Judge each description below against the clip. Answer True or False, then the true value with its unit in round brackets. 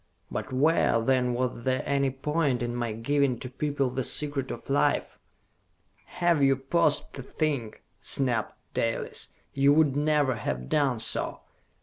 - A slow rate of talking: False (145 wpm)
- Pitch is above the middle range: False (135 Hz)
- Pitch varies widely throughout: False (2.9 semitones)